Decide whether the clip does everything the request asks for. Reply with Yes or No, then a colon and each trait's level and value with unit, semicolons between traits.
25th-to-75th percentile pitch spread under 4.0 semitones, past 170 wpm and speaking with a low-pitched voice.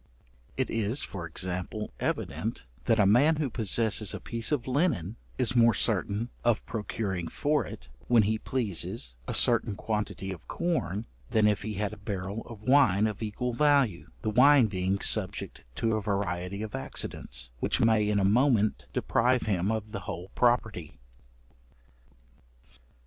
No: average, 3.5 semitones; average, 155 wpm; low, 110 Hz